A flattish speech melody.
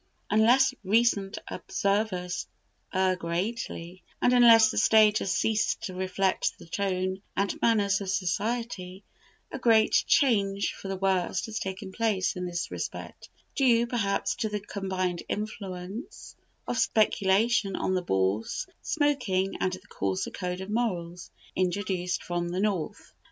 No: average, 3.1 semitones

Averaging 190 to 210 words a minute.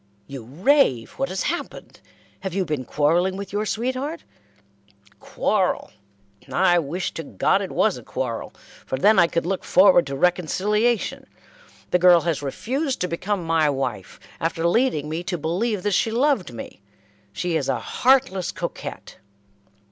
No: average, 155 wpm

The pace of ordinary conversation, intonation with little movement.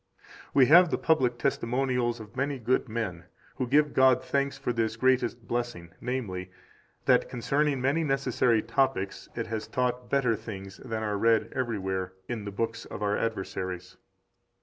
No: average, 165 wpm; average, 3.4 semitones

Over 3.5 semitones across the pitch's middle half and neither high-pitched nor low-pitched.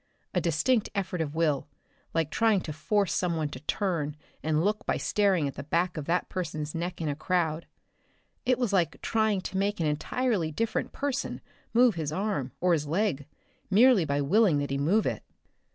Yes: average, 5.2 semitones; medium, 175 Hz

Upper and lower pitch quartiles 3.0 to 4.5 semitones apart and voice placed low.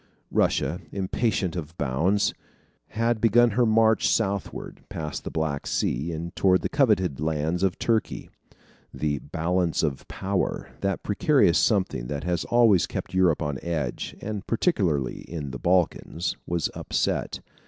No: average, 5.1 semitones; very low, 90 Hz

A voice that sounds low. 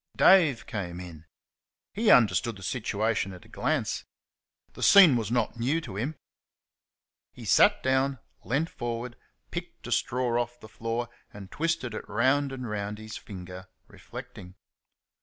Yes: low, 115 Hz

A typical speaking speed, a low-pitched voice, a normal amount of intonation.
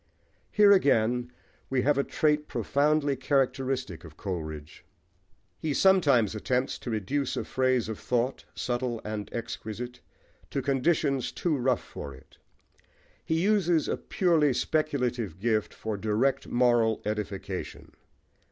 No: slow, 125 wpm; low, 125 Hz; average, 4.8 semitones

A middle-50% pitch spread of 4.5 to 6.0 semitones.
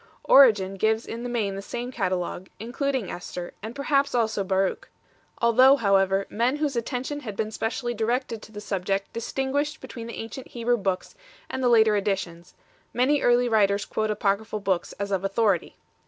No: average, 3.8 semitones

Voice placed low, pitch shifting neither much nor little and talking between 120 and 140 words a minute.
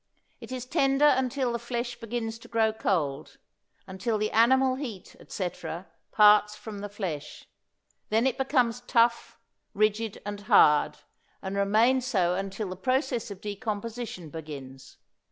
No: high, 220 Hz; average, 3.8 semitones; slow, 135 wpm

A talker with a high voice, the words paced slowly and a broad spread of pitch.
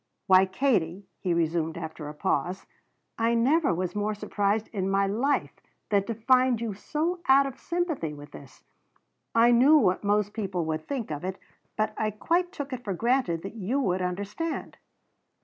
No: high, 210 Hz; average, 175 wpm; wide, 5.9 semitones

